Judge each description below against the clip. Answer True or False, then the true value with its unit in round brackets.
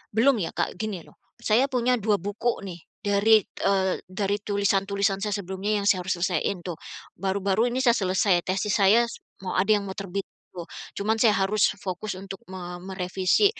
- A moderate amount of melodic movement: False (2.1 semitones)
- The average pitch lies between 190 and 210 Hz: True (200 Hz)